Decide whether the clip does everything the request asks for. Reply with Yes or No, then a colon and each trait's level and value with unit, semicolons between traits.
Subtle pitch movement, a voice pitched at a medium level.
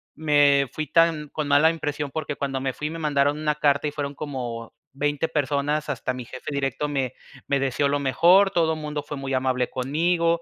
Yes: narrow, 2.1 semitones; medium, 145 Hz